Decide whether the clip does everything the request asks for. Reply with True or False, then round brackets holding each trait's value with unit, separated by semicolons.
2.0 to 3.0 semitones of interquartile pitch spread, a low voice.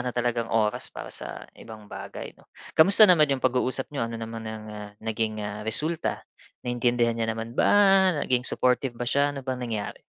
True (2.7 semitones; 120 Hz)